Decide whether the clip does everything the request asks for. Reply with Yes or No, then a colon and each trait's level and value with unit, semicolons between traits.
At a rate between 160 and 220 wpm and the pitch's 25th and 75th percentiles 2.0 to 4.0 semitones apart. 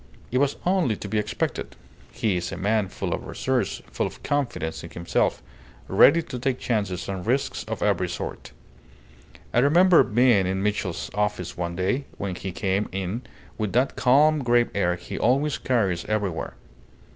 No: average, 170 wpm; average, 5.3 semitones